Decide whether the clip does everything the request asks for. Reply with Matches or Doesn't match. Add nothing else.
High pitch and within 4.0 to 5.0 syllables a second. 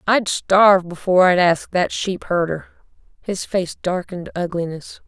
Doesn't match